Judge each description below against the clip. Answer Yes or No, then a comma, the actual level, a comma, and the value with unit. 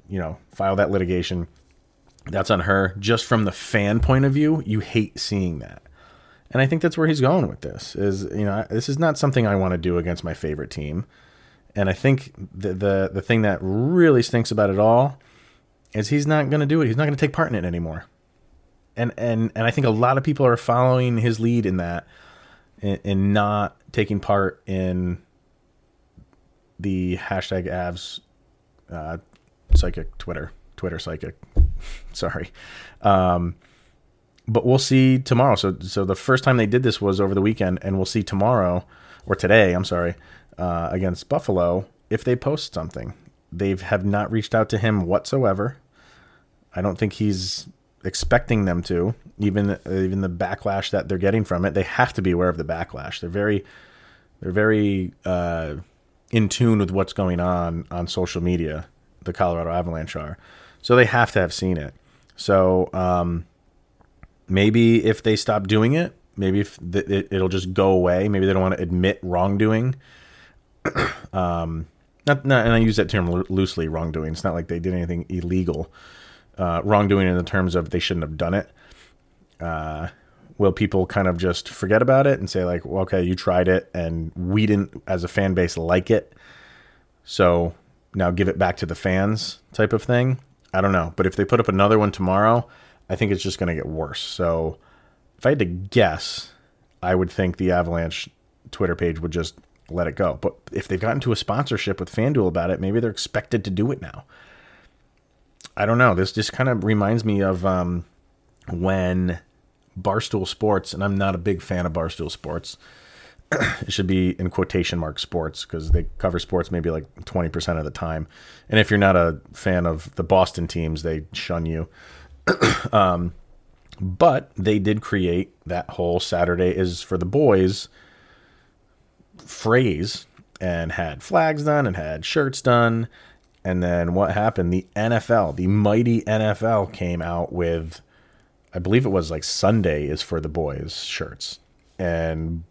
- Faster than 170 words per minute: Yes, average, 180 wpm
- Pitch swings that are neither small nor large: Yes, average, 3.8 semitones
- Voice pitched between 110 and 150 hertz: No, very low, 95 Hz